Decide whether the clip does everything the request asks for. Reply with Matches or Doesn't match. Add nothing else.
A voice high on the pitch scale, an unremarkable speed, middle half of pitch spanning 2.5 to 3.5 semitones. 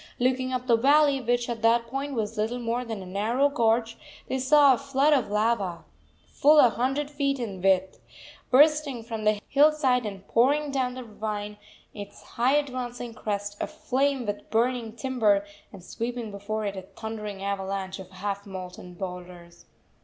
Doesn't match